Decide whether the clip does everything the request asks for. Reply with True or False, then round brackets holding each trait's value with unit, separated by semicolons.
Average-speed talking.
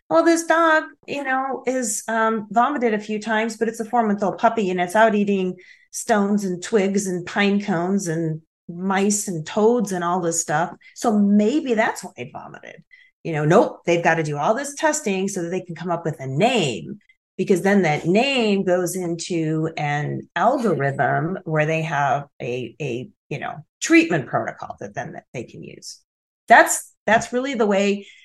True (185 wpm)